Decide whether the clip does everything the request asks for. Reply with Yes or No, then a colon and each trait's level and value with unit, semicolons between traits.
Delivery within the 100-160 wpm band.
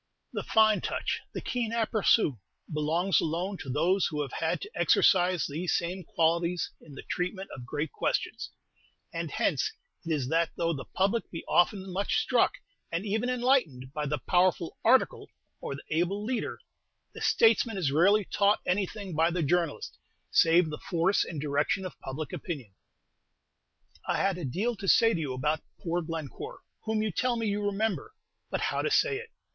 No: average, 175 wpm